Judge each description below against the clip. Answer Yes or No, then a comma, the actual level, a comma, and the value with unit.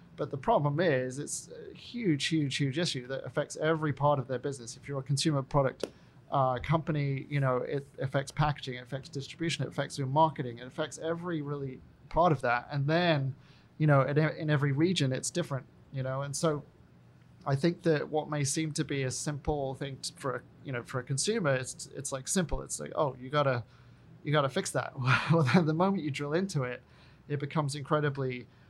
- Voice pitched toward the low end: No, medium, 145 Hz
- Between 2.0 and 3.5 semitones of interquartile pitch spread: Yes, average, 2.7 semitones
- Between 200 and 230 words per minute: Yes, fast, 205 wpm